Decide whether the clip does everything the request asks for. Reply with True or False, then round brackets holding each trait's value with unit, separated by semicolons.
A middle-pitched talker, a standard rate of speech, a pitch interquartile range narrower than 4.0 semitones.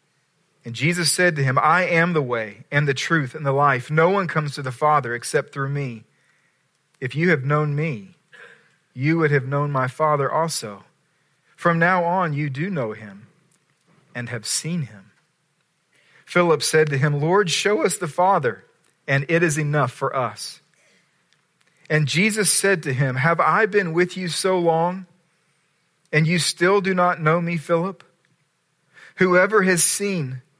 True (160 Hz; 165 wpm; 3.4 semitones)